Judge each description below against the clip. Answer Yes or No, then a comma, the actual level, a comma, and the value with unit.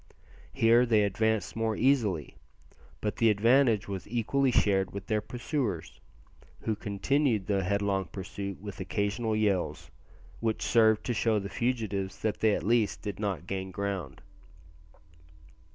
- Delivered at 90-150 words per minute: Yes, slow, 135 wpm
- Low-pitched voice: Yes, low, 105 Hz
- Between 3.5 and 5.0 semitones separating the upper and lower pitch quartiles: No, average, 2.7 semitones